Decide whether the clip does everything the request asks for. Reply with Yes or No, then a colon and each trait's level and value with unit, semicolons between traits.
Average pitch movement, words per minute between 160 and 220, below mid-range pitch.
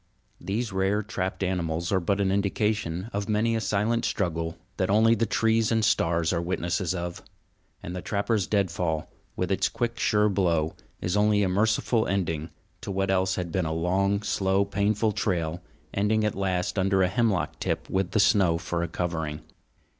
Yes: average, 3.2 semitones; average, 175 wpm; very low, 95 Hz